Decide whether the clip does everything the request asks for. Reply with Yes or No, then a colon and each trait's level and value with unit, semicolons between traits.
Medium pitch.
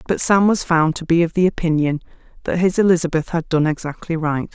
Yes: medium, 165 Hz